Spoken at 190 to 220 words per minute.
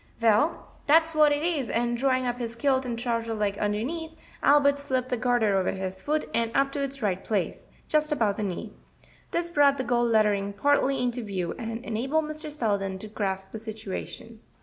Yes: average, 195 wpm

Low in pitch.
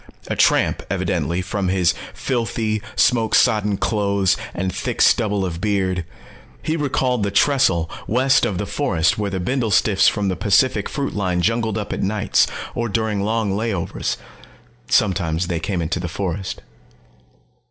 Yes: low, 100 Hz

